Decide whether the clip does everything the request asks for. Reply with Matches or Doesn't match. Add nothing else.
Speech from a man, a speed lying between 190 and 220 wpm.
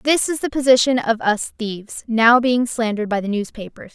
Doesn't match